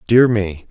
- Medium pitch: No, low, 105 Hz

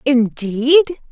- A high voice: Yes, very high, 265 Hz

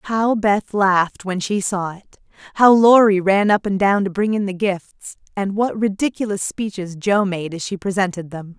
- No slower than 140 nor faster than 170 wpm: No, average, 195 wpm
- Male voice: No, female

